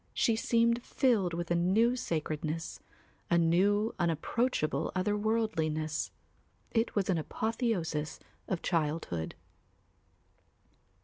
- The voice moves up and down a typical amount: No, wide, 5.8 semitones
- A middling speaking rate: No, slow, 90 wpm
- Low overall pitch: No, medium, 180 Hz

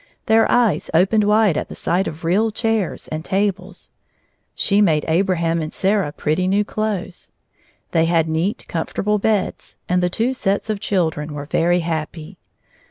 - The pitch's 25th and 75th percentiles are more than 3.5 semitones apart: Yes, average, 4.1 semitones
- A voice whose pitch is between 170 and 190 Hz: Yes, medium, 185 Hz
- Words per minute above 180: No, average, 160 wpm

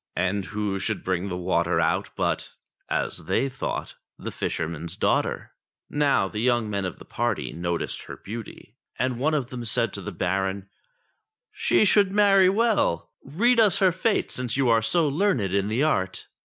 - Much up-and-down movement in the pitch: Yes, wide, 8.1 semitones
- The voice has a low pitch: Yes, low, 115 Hz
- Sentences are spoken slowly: No, average, 180 wpm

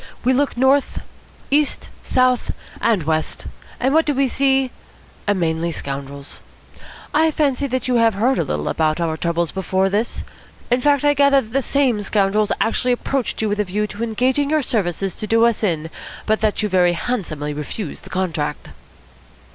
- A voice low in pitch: No, high, 215 Hz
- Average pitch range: No, wide, 7.0 semitones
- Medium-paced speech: Yes, average, 170 wpm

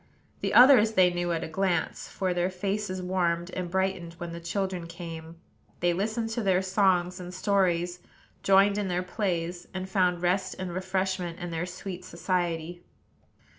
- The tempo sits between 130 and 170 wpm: Yes, average, 165 wpm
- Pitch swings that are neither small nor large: No, narrow, 1.6 semitones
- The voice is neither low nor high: Yes, medium, 180 Hz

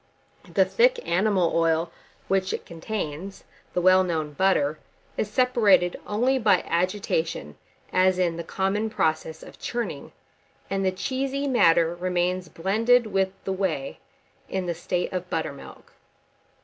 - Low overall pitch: No, medium, 185 Hz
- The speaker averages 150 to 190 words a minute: No, slow, 135 wpm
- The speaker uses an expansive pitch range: No, average, 3.8 semitones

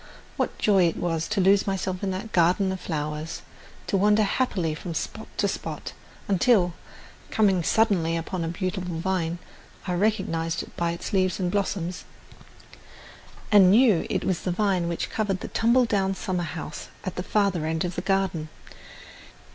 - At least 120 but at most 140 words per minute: No, average, 165 wpm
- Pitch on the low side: No, medium, 185 Hz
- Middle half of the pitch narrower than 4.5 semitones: Yes, average, 2.9 semitones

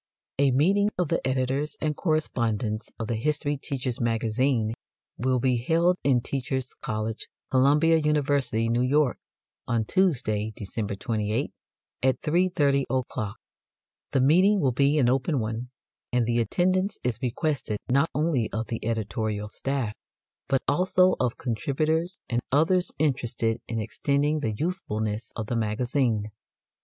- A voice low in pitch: Yes, low, 130 Hz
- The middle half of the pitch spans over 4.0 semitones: Yes, average, 4.9 semitones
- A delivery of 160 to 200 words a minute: No, slow, 135 wpm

